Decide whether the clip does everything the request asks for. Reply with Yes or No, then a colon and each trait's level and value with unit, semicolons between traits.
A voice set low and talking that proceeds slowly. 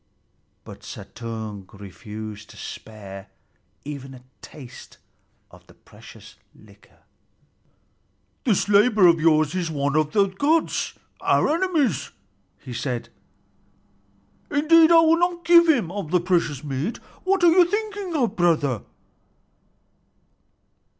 No: medium, 175 Hz; slow, 115 wpm